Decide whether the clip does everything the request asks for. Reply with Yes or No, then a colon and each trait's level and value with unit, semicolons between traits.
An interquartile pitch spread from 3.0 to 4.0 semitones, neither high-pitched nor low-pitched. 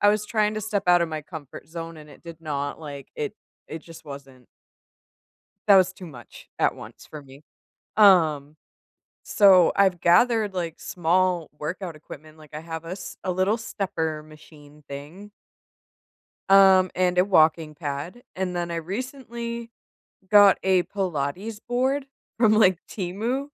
No: average, 4.6 semitones; medium, 175 Hz